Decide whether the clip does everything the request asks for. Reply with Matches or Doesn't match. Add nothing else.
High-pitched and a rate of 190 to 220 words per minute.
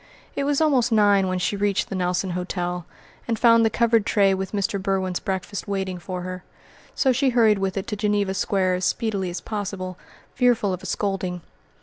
Matches